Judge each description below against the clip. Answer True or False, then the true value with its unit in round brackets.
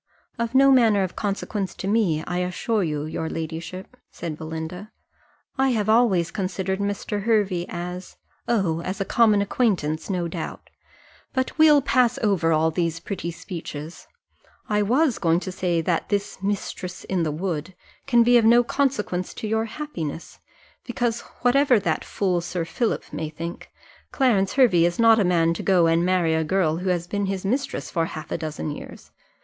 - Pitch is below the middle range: False (190 Hz)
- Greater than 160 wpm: True (175 wpm)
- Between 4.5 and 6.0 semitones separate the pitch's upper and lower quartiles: True (4.9 semitones)